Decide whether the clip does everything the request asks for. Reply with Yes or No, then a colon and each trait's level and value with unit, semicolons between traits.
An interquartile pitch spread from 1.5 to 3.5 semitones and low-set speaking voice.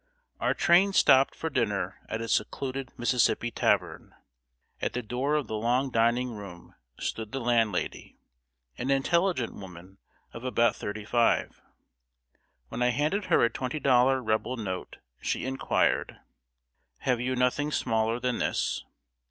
Yes: average, 2.9 semitones; low, 125 Hz